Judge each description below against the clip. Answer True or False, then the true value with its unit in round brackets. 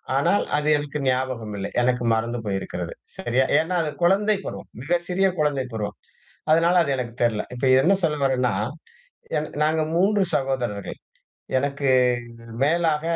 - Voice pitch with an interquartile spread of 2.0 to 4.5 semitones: False (4.9 semitones)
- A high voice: False (140 Hz)